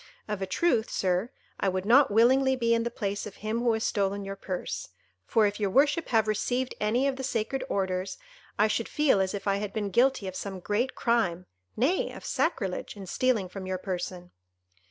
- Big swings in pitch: No, average, 4.0 semitones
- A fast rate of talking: No, average, 195 wpm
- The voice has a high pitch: Yes, high, 210 Hz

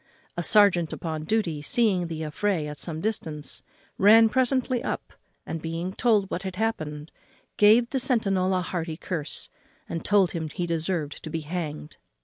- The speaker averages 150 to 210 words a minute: Yes, average, 160 wpm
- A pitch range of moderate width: Yes, average, 4.9 semitones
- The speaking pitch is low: No, medium, 180 Hz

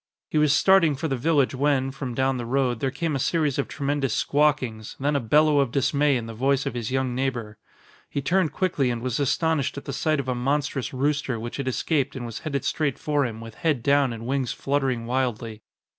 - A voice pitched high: No, low, 135 Hz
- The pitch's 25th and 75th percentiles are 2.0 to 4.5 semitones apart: Yes, average, 2.9 semitones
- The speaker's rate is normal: No, fast, 220 wpm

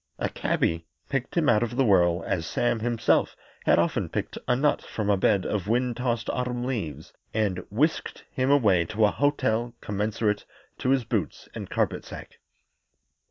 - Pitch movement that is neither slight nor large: Yes, average, 3.5 semitones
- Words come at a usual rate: Yes, average, 170 wpm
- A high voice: No, low, 115 Hz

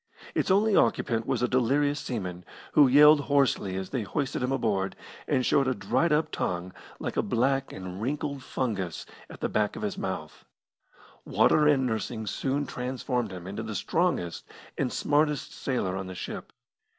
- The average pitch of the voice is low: Yes, low, 125 Hz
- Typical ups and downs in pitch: No, wide, 6.6 semitones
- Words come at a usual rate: Yes, average, 170 wpm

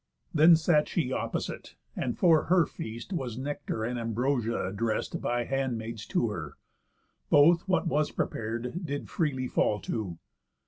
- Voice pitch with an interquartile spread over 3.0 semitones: Yes, average, 5.1 semitones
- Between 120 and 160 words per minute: Yes, average, 140 wpm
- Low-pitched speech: Yes, low, 125 Hz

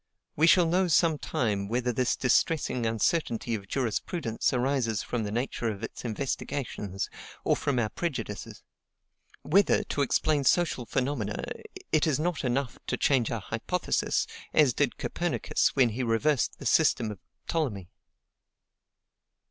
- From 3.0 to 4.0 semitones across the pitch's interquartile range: No, average, 5.1 semitones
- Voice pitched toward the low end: Yes, low, 125 Hz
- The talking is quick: No, average, 140 wpm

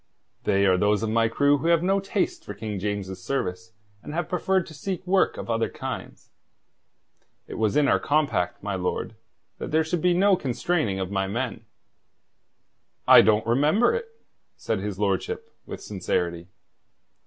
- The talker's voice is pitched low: Yes, low, 115 Hz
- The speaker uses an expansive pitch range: Yes, wide, 8.4 semitones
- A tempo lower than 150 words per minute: No, average, 165 wpm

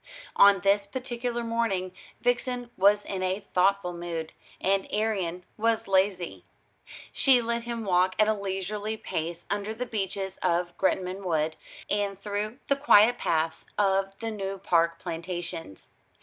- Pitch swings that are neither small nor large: Yes, average, 3.3 semitones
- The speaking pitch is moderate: No, high, 195 Hz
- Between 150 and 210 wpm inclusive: No, average, 140 wpm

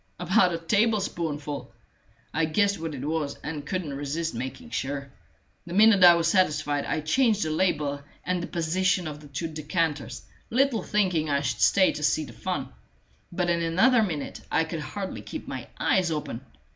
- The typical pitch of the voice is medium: Yes, medium, 165 Hz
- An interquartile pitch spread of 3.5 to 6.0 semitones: Yes, average, 3.9 semitones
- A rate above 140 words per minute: Yes, average, 175 wpm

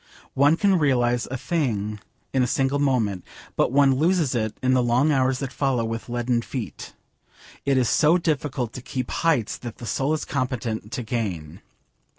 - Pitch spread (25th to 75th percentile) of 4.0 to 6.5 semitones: No, average, 3.2 semitones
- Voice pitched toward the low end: Yes, low, 130 Hz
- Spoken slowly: No, average, 175 wpm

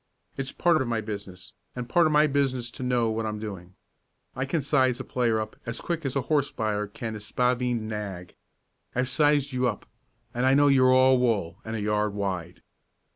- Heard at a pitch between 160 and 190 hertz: No, low, 120 Hz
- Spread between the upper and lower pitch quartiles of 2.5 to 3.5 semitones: No, average, 3.9 semitones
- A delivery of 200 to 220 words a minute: Yes, fast, 205 wpm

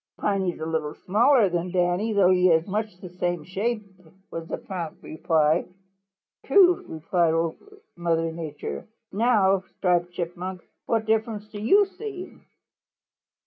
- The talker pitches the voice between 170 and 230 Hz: Yes, medium, 185 Hz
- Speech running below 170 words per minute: Yes, average, 140 wpm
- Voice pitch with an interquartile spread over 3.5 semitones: Yes, average, 4.2 semitones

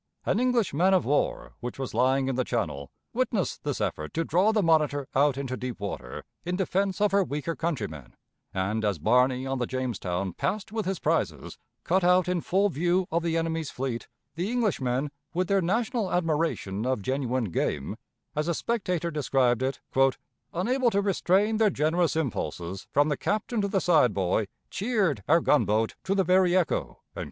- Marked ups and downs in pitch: Yes, wide, 6.8 semitones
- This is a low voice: No, medium, 155 Hz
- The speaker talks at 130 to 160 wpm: No, average, 180 wpm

